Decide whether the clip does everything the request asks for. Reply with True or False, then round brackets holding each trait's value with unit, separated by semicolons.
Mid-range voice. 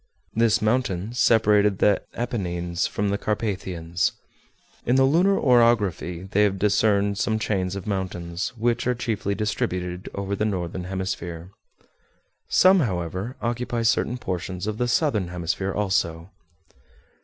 False (100 Hz)